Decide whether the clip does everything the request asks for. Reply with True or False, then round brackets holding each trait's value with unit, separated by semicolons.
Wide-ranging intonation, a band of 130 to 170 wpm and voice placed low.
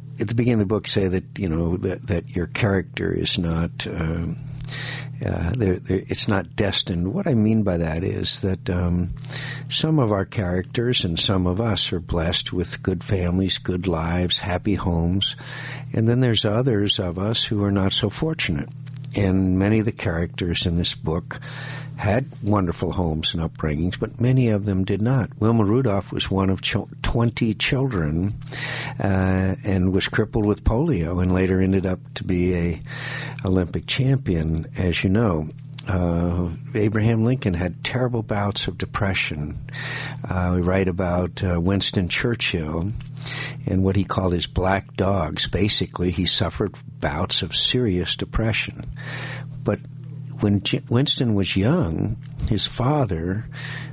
True (6.2 semitones; 155 wpm; 105 Hz)